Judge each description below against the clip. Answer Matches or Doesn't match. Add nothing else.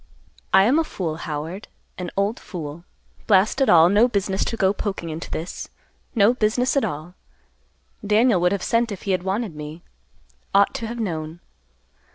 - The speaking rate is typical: Matches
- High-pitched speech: Matches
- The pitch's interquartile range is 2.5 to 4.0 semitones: Doesn't match